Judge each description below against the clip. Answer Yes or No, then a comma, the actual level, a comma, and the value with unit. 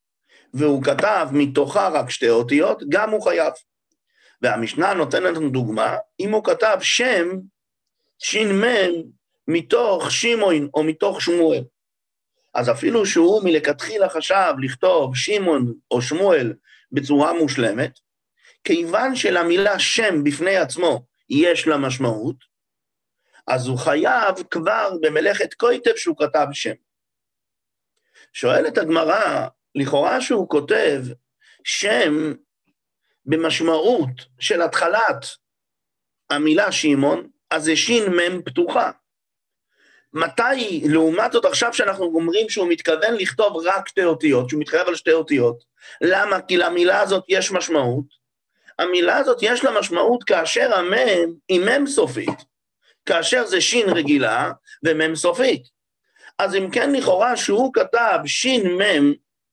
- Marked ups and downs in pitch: Yes, wide, 7.3 semitones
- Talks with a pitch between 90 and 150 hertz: No, medium, 175 Hz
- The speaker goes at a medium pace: No, slow, 115 wpm